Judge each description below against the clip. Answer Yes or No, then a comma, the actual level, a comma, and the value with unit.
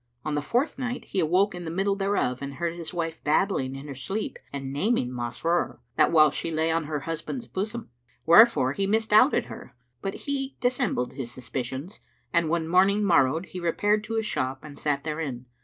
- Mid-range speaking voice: Yes, medium, 165 Hz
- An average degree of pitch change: No, wide, 6.3 semitones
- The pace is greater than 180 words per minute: Yes, average, 190 wpm